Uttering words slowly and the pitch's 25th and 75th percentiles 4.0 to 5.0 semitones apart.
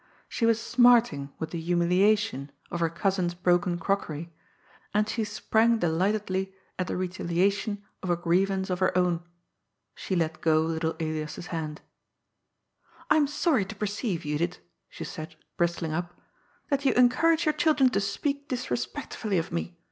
No: average, 155 wpm; average, 4.6 semitones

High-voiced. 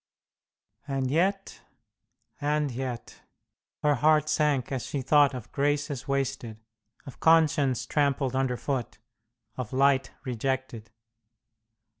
No: low, 135 Hz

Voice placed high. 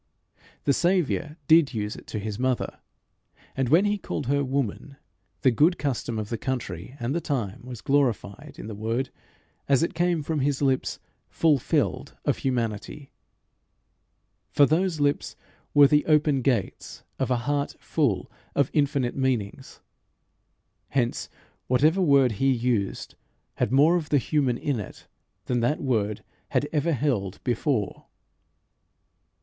No: low, 135 Hz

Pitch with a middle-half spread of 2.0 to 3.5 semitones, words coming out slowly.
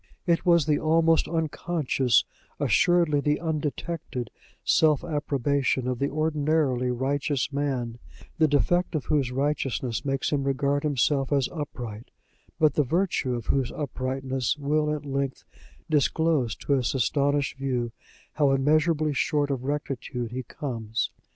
Yes: average, 2.8 semitones; slow, 130 wpm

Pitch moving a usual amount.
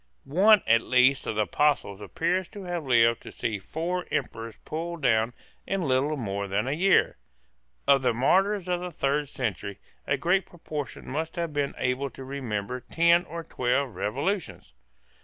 No: wide, 6.5 semitones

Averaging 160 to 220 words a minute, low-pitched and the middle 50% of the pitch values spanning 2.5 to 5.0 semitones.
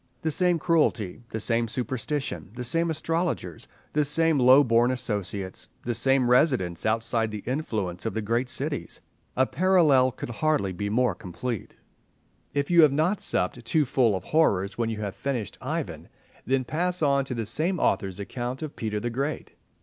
No: average, 170 wpm; low, 125 Hz; wide, 5.5 semitones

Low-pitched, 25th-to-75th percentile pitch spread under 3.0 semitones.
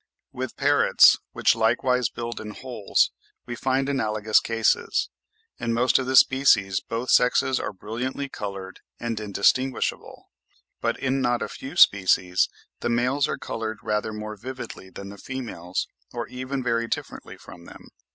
No: low, 120 Hz; average, 3.3 semitones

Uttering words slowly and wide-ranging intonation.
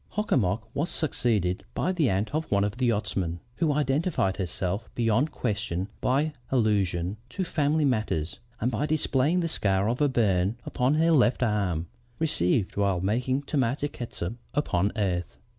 No: average, 160 wpm; wide, 6.9 semitones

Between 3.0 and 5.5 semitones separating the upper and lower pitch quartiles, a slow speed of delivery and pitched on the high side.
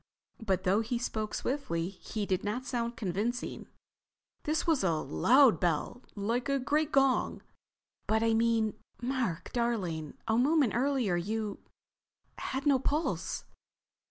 Yes: average, 4.7 semitones; slow, 120 wpm; high, 230 Hz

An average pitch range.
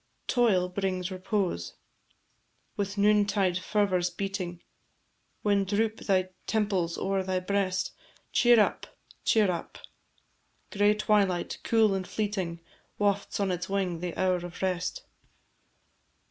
No: narrow, 2.2 semitones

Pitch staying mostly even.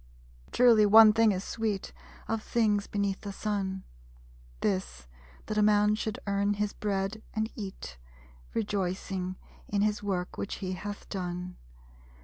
Yes: narrow, 2.0 semitones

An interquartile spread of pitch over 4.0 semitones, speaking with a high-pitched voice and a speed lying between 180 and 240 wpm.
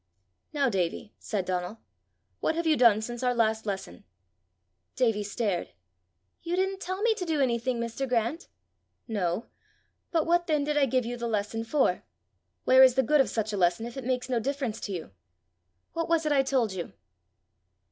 Yes: average, 5.0 semitones; high, 245 Hz; average, 185 wpm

